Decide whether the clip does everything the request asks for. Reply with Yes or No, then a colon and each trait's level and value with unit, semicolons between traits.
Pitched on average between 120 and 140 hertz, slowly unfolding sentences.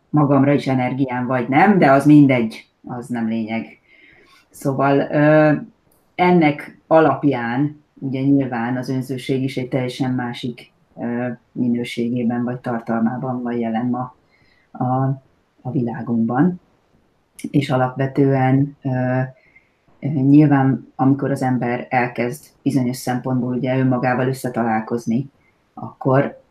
Yes: low, 130 Hz; slow, 100 wpm